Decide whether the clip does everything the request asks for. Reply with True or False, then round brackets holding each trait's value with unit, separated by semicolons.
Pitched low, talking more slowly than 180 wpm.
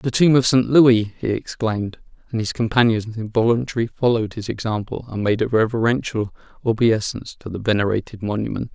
True (115 Hz; 160 wpm)